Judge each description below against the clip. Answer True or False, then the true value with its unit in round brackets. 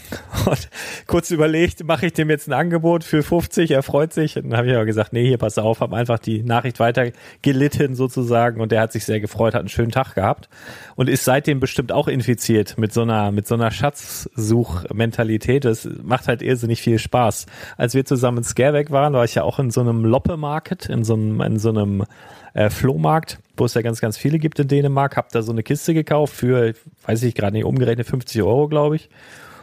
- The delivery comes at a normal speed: False (220 wpm)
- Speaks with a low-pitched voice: True (125 Hz)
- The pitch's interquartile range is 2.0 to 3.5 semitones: False (4.1 semitones)